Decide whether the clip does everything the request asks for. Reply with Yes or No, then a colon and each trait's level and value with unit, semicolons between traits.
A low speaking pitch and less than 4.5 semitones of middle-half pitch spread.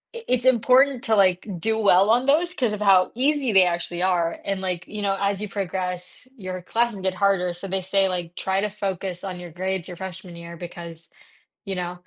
No: high, 190 Hz; average, 2.9 semitones